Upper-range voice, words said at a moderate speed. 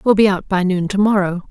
No: high, 195 Hz; fast, 240 wpm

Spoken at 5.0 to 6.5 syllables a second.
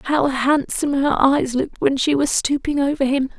Yes: 5.1 syllables/s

